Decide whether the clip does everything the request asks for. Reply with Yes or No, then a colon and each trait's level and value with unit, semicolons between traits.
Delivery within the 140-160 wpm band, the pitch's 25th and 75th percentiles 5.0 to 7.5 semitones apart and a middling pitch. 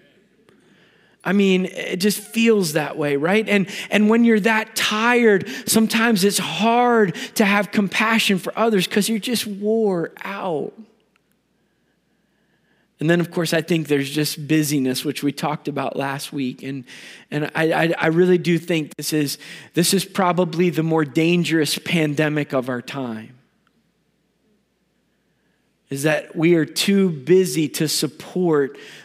Yes: average, 145 wpm; wide, 5.5 semitones; medium, 175 Hz